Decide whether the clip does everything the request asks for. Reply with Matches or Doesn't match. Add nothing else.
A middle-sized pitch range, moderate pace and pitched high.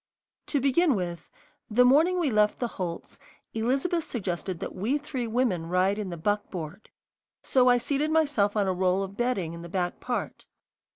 Doesn't match